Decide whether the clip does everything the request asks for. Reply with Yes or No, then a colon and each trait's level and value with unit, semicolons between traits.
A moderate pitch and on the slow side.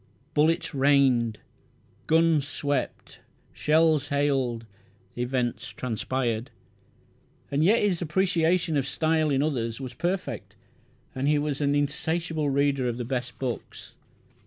Yes: medium, 145 Hz; slow, 115 wpm